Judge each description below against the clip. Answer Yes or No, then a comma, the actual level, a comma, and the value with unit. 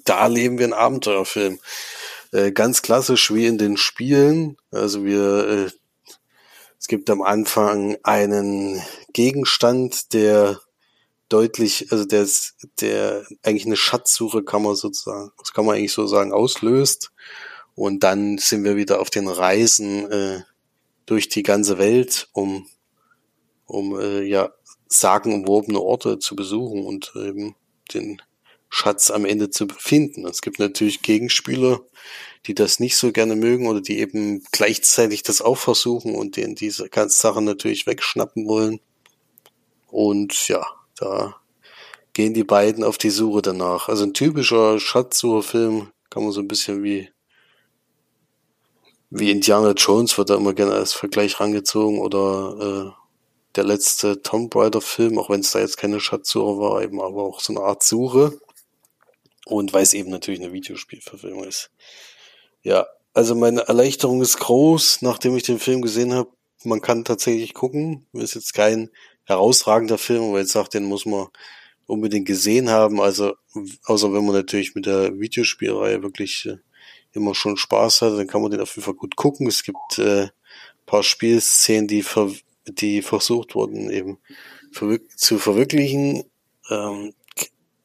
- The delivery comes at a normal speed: Yes, average, 150 wpm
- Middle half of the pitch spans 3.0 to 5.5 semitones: No, narrow, 2.5 semitones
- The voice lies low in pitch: Yes, low, 105 Hz